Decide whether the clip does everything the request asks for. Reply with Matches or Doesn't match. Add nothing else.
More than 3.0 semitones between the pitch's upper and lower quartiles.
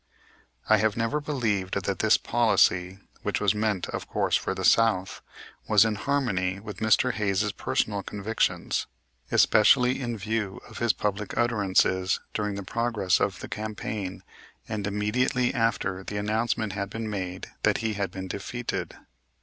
Doesn't match